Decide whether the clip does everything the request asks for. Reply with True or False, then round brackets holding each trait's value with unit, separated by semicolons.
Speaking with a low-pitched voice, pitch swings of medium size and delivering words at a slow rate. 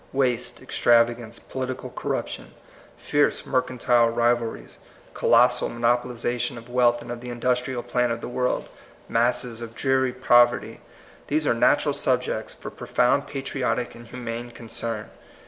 False (120 Hz; 1.1 semitones; 130 wpm)